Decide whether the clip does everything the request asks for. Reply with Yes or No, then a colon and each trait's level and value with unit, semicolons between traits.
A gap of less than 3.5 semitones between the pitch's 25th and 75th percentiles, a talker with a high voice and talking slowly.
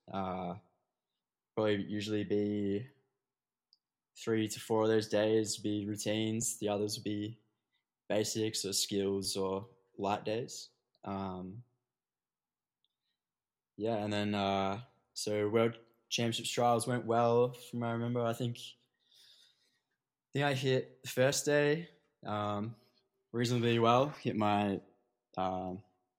No: average, 2.9 semitones; low, 110 Hz; slow, 120 wpm